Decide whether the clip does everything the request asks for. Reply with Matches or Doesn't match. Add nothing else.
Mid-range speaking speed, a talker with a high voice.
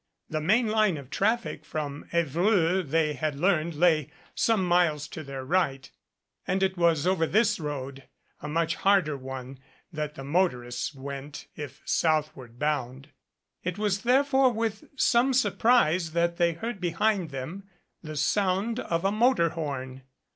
Doesn't match